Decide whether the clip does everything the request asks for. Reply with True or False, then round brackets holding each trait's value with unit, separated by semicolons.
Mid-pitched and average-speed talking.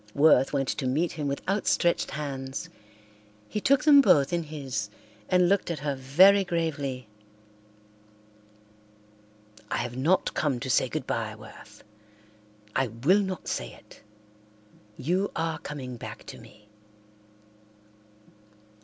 False (150 Hz; 125 wpm)